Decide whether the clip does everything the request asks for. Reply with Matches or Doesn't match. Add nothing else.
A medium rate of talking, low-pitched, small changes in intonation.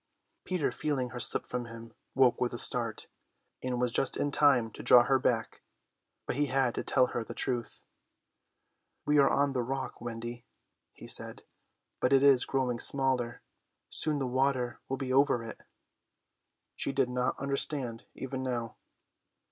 Matches